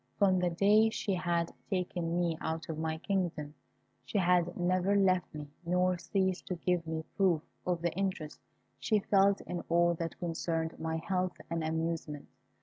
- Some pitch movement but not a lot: No, narrow, 2.2 semitones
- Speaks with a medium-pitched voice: Yes, medium, 175 Hz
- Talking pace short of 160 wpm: No, average, 165 wpm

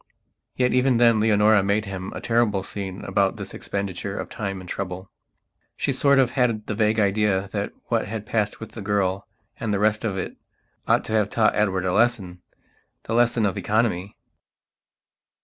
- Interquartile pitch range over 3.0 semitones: No, narrow, 2.4 semitones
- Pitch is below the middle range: Yes, low, 105 Hz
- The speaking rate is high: No, average, 175 wpm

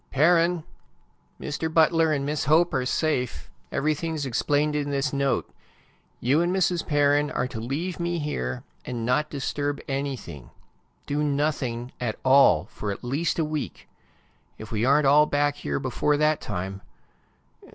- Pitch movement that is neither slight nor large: Yes, average, 3.3 semitones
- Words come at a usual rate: Yes, average, 150 wpm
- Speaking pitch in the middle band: Yes, medium, 145 Hz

